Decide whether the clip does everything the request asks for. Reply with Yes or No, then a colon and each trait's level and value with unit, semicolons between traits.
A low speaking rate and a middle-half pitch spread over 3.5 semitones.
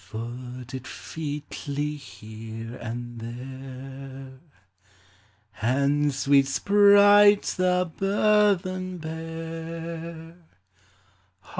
Yes: slow, 60 wpm; average, 5.1 semitones